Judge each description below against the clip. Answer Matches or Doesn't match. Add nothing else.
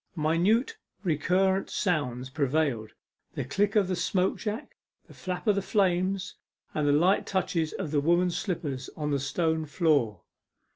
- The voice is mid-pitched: Matches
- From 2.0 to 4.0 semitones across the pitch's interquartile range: Doesn't match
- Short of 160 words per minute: Matches